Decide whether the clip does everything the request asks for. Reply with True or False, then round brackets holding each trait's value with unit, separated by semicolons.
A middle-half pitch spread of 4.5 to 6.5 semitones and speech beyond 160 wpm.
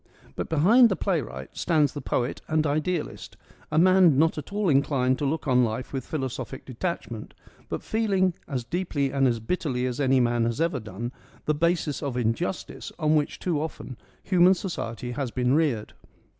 True (5.1 semitones; 180 wpm)